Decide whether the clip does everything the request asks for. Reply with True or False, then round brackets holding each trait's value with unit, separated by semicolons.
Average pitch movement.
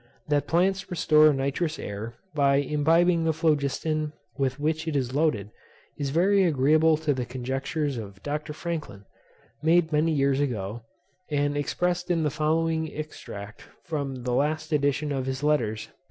True (3.0 semitones)